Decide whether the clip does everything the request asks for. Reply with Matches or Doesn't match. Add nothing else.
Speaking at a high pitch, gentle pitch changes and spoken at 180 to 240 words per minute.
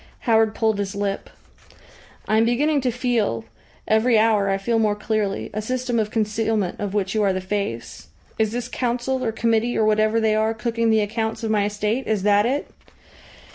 Matches